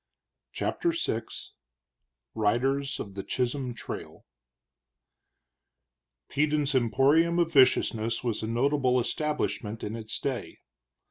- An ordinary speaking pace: No, slow, 95 wpm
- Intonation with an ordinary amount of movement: Yes, average, 4.3 semitones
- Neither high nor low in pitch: No, low, 130 Hz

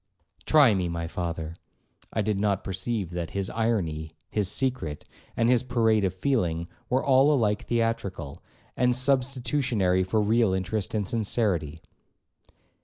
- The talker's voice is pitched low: Yes, low, 105 Hz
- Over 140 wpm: No, slow, 135 wpm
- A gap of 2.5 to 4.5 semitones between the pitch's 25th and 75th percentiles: No, average, 5.0 semitones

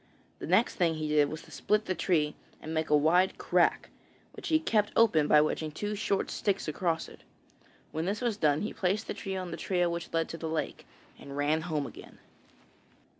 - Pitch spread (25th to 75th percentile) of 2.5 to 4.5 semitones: Yes, average, 4.1 semitones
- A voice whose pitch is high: No, medium, 165 Hz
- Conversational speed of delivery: No, fast, 210 wpm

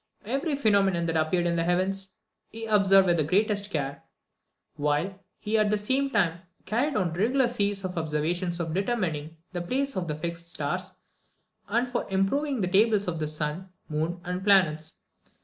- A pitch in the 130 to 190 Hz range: Yes, medium, 185 Hz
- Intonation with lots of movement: No, average, 4.1 semitones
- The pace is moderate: Yes, average, 170 wpm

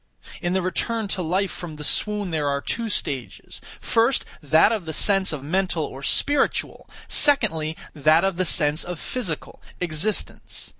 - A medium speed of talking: Yes, average, 160 wpm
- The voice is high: No, medium, 180 Hz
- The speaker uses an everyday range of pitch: Yes, average, 4.9 semitones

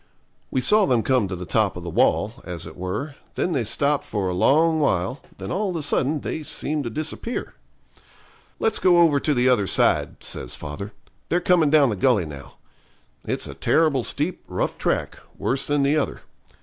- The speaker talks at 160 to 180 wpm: No, average, 195 wpm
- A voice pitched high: No, low, 135 Hz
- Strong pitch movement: Yes, wide, 7.6 semitones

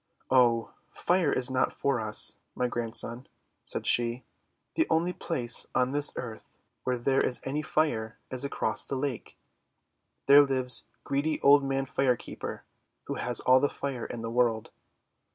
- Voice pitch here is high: No, low, 130 Hz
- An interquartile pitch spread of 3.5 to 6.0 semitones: No, average, 2.8 semitones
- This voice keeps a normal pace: Yes, average, 155 wpm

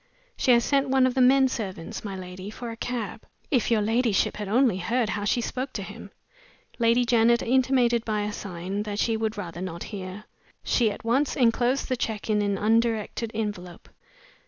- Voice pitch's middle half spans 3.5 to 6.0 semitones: No, average, 3.1 semitones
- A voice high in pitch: Yes, high, 225 Hz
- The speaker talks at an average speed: Yes, average, 190 wpm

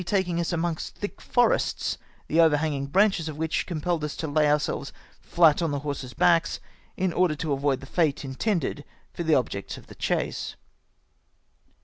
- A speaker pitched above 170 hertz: No, medium, 160 Hz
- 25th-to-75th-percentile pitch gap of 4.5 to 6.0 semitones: No, average, 3.1 semitones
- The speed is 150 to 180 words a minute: Yes, average, 170 wpm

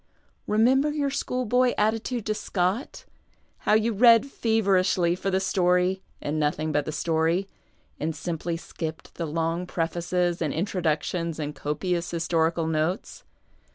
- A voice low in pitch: No, medium, 180 Hz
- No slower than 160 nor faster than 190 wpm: No, slow, 135 wpm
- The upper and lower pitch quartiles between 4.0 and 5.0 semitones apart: Yes, average, 4.6 semitones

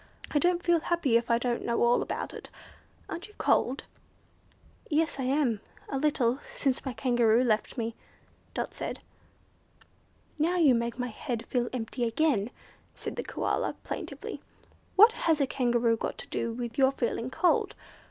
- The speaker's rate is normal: Yes, average, 160 wpm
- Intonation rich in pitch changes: No, average, 4.3 semitones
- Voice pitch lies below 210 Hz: No, very high, 250 Hz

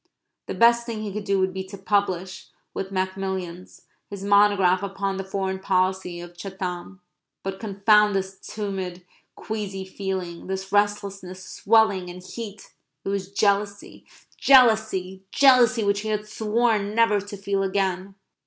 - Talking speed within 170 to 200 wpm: No, average, 145 wpm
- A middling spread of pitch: No, narrow, 1.7 semitones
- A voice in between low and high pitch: No, high, 195 Hz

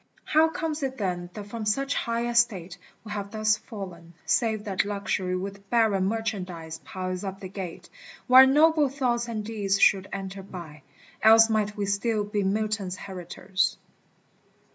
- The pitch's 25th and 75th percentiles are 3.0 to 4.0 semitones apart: Yes, average, 3.3 semitones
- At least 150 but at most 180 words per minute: Yes, average, 155 wpm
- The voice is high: Yes, high, 205 Hz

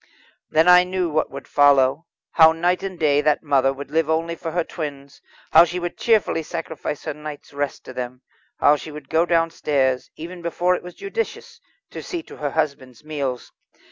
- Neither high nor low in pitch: Yes, medium, 155 Hz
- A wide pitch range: No, average, 3.5 semitones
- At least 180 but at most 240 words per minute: Yes, average, 190 wpm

